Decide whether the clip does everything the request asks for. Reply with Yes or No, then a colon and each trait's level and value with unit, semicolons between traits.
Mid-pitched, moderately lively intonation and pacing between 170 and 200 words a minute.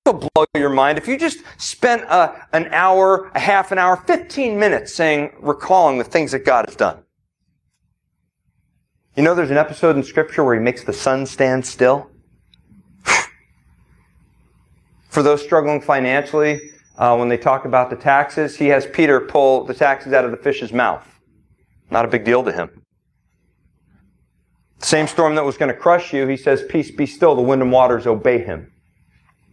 Yes: medium, 145 Hz; average, 3.8 semitones; average, 175 wpm